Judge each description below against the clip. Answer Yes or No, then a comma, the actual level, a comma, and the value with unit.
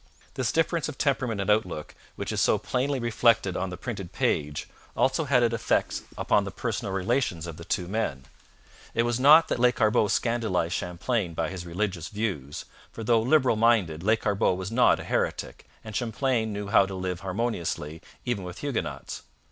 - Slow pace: No, average, 175 wpm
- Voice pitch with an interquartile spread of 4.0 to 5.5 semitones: Yes, average, 4.9 semitones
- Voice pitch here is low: Yes, low, 105 Hz